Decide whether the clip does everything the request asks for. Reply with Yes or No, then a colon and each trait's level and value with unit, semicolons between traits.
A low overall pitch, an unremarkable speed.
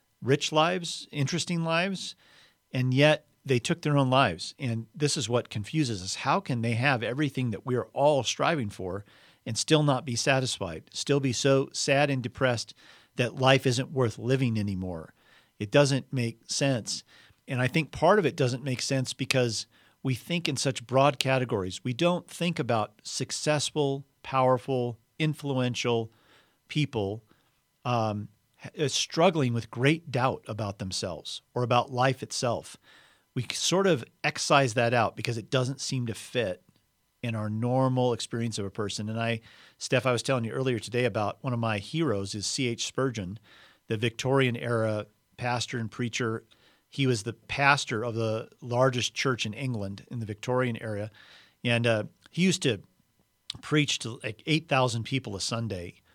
Yes: low, 125 Hz; average, 165 wpm